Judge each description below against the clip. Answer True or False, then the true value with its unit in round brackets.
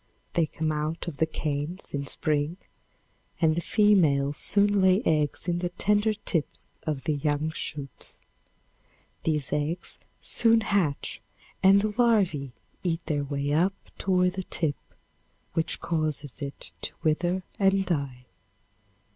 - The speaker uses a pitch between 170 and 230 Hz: False (160 Hz)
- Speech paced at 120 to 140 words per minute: True (135 wpm)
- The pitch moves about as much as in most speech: True (4.4 semitones)